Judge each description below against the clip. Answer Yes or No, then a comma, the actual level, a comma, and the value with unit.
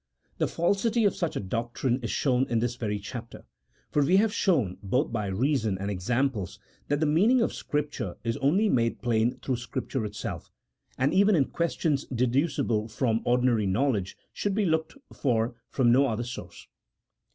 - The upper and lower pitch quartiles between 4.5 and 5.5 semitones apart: Yes, average, 5.0 semitones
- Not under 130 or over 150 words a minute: No, average, 175 wpm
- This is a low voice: Yes, low, 125 Hz